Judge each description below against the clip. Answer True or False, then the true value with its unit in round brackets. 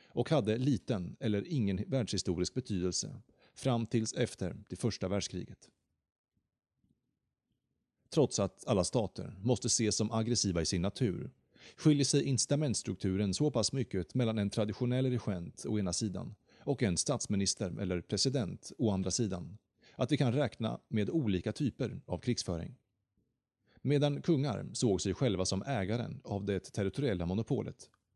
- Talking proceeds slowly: False (140 wpm)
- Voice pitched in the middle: False (110 Hz)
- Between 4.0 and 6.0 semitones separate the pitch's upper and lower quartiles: True (4.8 semitones)